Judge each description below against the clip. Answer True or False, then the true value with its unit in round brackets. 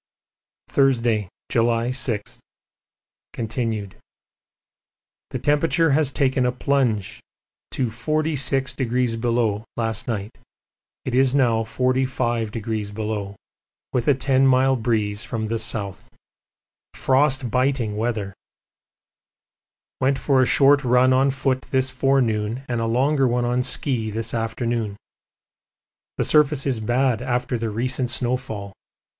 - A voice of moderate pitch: False (125 Hz)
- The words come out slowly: True (110 wpm)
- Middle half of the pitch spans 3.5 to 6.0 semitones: False (2.8 semitones)